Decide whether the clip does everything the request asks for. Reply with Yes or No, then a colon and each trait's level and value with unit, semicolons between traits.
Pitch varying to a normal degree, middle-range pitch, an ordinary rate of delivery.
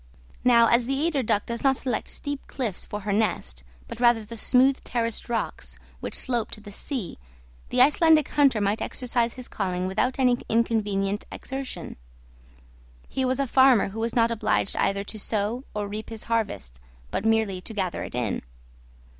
No: average, 3.7 semitones; high, 230 Hz; average, 175 wpm